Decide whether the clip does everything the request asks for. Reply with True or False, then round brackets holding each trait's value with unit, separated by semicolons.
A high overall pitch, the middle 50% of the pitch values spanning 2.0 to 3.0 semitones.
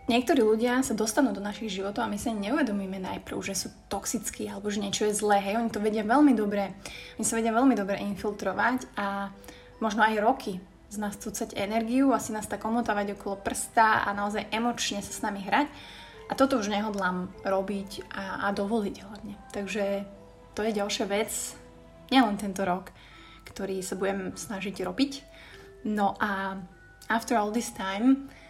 True (210 Hz; 2.4 semitones)